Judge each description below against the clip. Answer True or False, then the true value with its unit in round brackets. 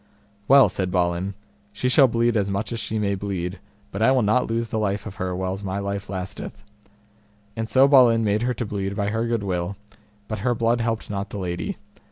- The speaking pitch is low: True (105 Hz)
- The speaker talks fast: True (215 wpm)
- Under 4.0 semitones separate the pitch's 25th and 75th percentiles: True (3.1 semitones)